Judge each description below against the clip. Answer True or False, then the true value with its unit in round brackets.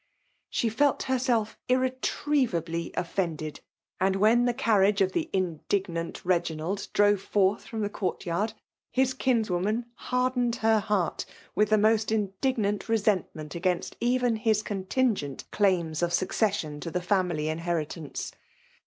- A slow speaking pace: True (130 wpm)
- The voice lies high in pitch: True (205 Hz)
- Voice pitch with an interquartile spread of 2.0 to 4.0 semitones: False (4.7 semitones)